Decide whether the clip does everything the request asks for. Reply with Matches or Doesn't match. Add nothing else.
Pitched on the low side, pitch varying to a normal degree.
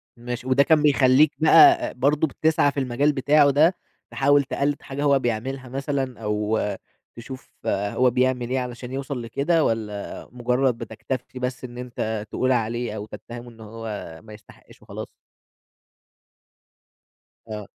Matches